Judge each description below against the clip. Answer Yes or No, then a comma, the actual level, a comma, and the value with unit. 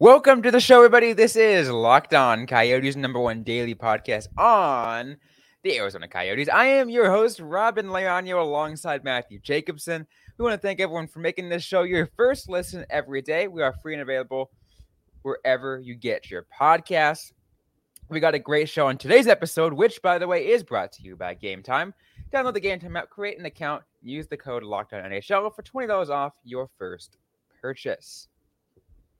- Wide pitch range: Yes, wide, 7.5 semitones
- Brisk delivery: No, average, 180 wpm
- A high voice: No, medium, 160 Hz